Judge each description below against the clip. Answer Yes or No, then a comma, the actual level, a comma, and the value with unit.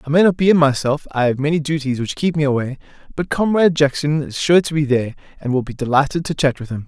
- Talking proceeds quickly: Yes, fast, 245 wpm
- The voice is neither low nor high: Yes, medium, 145 Hz